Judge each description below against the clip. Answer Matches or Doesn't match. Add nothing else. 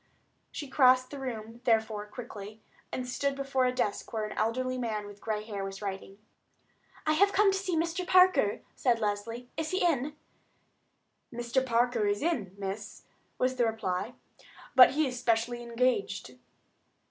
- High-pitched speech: Matches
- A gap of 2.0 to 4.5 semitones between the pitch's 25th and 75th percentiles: Matches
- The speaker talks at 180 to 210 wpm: Doesn't match